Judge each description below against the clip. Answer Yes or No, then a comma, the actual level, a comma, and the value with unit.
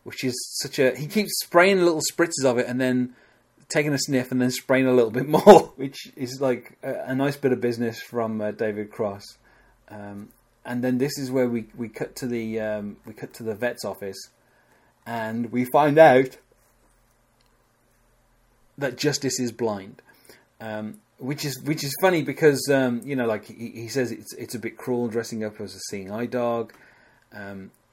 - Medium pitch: No, low, 125 Hz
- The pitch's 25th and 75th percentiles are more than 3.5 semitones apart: No, average, 2.9 semitones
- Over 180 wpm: Yes, average, 190 wpm